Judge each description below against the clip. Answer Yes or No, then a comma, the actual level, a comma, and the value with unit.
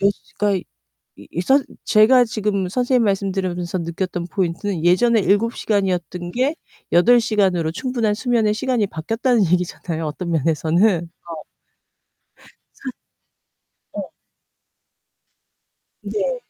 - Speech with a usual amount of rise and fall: Yes, average, 4.8 semitones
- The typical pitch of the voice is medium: No, high, 195 Hz